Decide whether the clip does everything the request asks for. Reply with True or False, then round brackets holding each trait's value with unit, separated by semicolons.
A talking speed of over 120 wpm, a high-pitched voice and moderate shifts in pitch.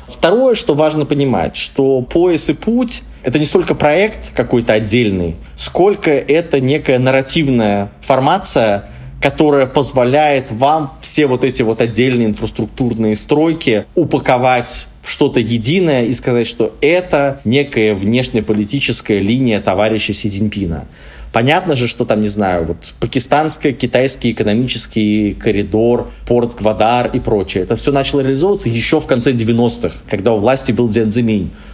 False (130 wpm; 125 Hz; 4.5 semitones)